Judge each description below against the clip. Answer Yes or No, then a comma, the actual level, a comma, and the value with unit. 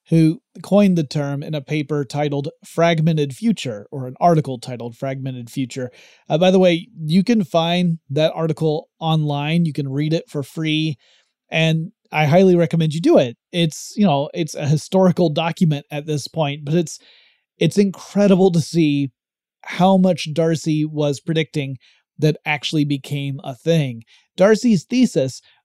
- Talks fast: No, average, 155 wpm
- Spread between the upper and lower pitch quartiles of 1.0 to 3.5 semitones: Yes, average, 3.2 semitones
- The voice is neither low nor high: Yes, medium, 160 Hz